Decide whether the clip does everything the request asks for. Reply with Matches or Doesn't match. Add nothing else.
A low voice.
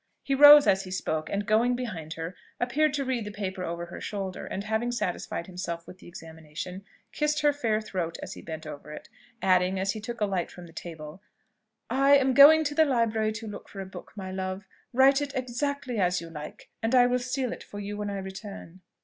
Doesn't match